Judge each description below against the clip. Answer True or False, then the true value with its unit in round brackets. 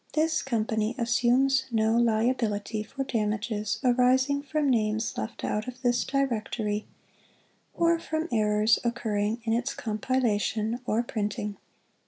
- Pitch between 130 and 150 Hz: False (235 Hz)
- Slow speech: True (125 wpm)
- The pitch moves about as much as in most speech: True (3.3 semitones)